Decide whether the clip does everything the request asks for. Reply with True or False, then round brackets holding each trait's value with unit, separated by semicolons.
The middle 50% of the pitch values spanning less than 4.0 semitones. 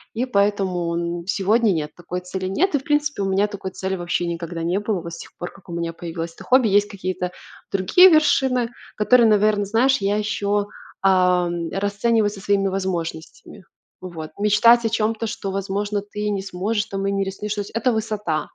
True (2.9 semitones)